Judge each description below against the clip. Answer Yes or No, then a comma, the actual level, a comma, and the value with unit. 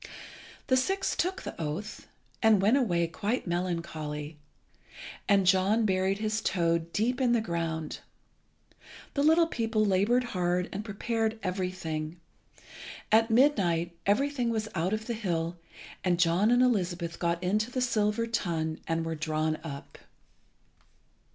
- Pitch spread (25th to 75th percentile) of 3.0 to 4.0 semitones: No, average, 5.0 semitones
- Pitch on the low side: No, high, 195 Hz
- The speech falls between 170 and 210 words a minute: No, slow, 135 wpm